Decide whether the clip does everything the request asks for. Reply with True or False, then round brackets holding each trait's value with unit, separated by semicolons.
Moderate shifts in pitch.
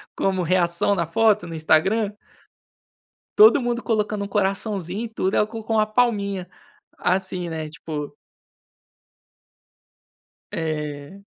True (4.2 semitones)